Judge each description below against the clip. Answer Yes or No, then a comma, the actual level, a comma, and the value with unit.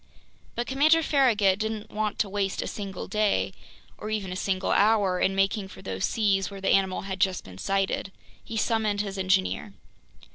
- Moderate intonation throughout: No, narrow, 2.1 semitones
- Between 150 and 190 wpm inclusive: Yes, average, 180 wpm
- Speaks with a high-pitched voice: Yes, high, 200 Hz